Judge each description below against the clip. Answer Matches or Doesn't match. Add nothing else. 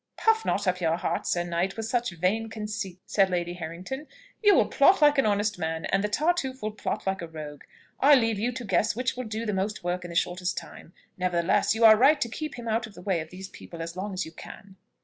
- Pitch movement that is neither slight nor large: Matches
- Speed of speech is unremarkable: Doesn't match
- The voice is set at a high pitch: Matches